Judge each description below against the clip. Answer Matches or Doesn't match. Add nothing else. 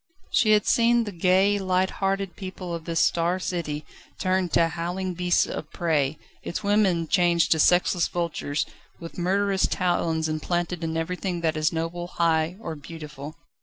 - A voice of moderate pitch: Matches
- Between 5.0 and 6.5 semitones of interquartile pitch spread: Doesn't match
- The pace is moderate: Matches